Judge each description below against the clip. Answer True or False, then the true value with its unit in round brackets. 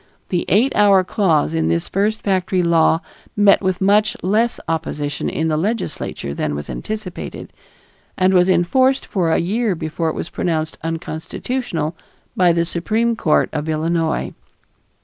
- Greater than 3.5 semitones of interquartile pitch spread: True (4.3 semitones)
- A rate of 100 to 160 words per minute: True (150 wpm)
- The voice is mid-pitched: True (175 Hz)